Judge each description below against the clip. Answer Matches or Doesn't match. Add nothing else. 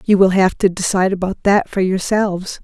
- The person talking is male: Doesn't match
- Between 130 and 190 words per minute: Doesn't match